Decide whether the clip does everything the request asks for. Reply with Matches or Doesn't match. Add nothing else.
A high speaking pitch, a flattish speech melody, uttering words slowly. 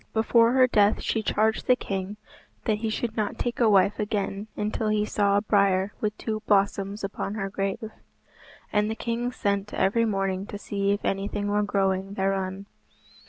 Doesn't match